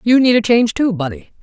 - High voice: Yes, high, 210 Hz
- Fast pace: Yes, fast, 250 wpm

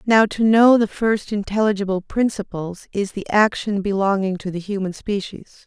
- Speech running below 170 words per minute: Yes, average, 160 wpm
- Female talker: Yes, female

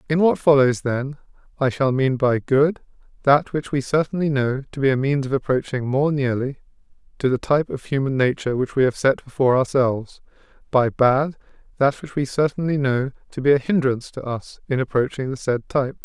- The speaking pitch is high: No, low, 135 Hz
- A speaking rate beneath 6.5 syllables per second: Yes, 5.6 syllables/s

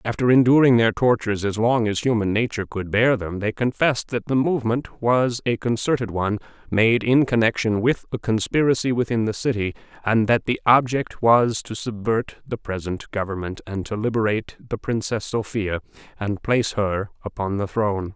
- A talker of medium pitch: No, low, 110 Hz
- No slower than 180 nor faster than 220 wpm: No, average, 170 wpm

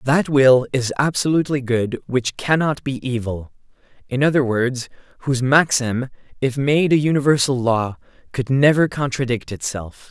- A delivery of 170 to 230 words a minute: No, slow, 135 wpm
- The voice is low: Yes, low, 130 Hz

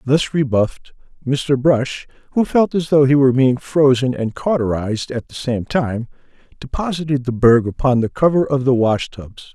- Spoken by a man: Yes, male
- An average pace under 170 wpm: No, average, 175 wpm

